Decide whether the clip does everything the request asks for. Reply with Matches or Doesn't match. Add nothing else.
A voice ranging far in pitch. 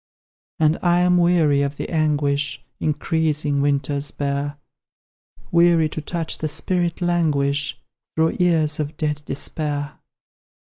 Doesn't match